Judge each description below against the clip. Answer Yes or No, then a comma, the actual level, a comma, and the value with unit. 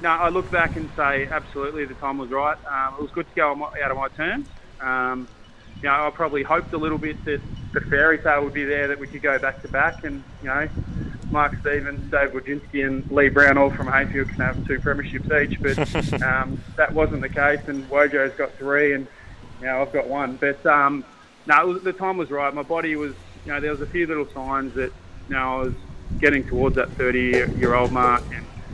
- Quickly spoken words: Yes, fast, 225 wpm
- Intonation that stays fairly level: Yes, narrow, 2.1 semitones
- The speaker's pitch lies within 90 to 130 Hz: No, medium, 140 Hz